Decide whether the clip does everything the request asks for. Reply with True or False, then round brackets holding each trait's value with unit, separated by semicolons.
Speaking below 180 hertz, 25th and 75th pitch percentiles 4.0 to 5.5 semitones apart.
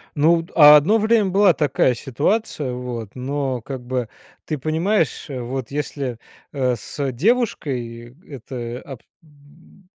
True (140 Hz; 4.5 semitones)